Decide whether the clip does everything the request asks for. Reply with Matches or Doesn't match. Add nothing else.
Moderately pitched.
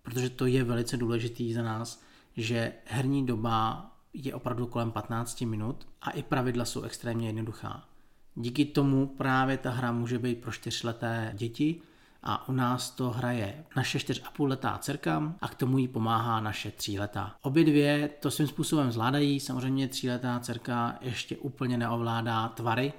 Doesn't match